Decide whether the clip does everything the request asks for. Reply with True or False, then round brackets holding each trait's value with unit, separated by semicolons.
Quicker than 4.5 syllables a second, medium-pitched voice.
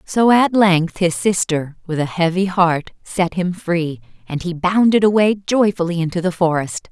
False (4.4 syllables/s; 180 Hz)